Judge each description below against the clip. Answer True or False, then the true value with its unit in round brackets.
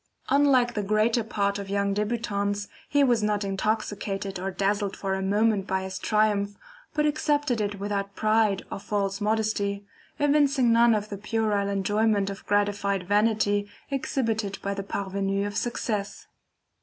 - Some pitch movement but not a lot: False (2.0 semitones)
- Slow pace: False (150 wpm)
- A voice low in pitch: False (205 Hz)